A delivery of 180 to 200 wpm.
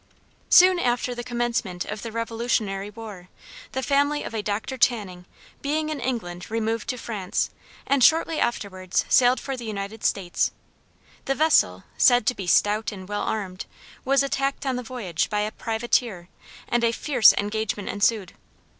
No: average, 160 wpm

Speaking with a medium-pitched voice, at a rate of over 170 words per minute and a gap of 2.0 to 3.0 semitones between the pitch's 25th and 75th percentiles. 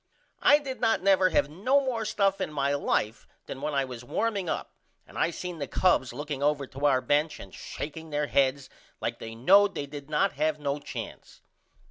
No: medium, 150 Hz; average, 200 wpm; wide, 5.5 semitones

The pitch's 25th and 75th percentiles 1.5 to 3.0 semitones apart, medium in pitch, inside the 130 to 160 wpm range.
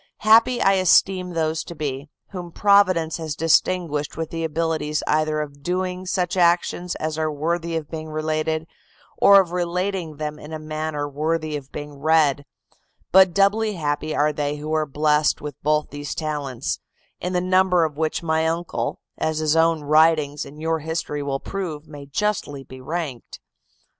No: average, 2.7 semitones; medium, 160 Hz; average, 170 wpm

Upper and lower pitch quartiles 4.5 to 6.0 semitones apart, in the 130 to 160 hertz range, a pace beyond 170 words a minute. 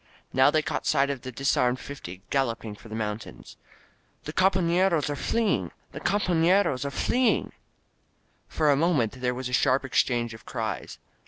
No: wide, 5.6 semitones; low, 135 Hz; average, 160 wpm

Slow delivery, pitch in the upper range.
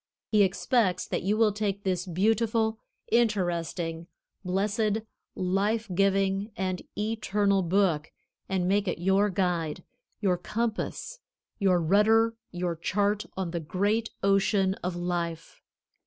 Yes: slow, 120 wpm; high, 195 Hz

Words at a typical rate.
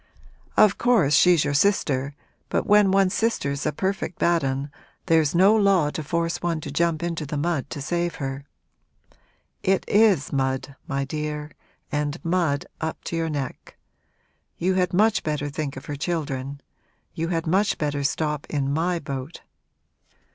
Yes: average, 160 wpm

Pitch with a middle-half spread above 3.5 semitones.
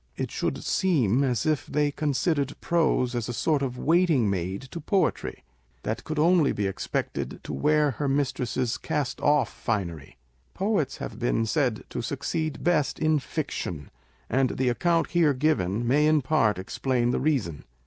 Yes: average, 4.5 semitones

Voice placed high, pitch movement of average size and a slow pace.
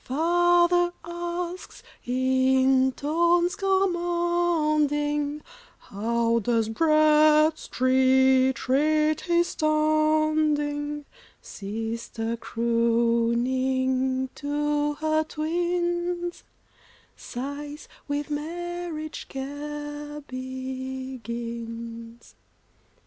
Yes: very high, 295 Hz; average, 3.4 semitones; slow, 55 wpm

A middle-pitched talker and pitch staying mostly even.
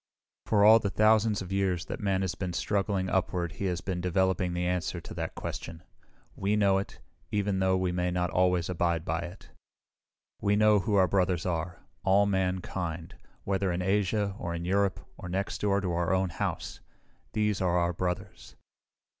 No: very low, 95 Hz; narrow, 2.1 semitones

